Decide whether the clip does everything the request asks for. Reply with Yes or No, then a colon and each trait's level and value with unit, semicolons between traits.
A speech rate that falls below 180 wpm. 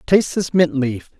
No: average, 200 wpm